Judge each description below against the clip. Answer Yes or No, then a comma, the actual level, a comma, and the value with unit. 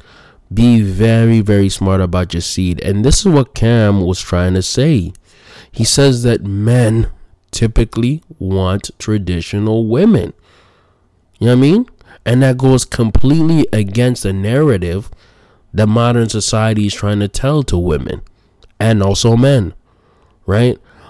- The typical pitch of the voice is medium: No, low, 110 Hz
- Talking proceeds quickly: No, average, 140 wpm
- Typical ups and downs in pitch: Yes, average, 4.5 semitones